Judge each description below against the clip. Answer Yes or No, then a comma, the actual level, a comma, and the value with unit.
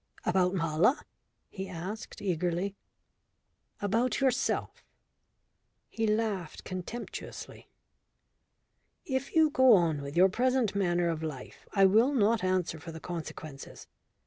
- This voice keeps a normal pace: No, slow, 115 wpm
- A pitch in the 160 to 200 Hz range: Yes, high, 190 Hz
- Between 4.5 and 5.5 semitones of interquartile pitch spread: Yes, average, 5.0 semitones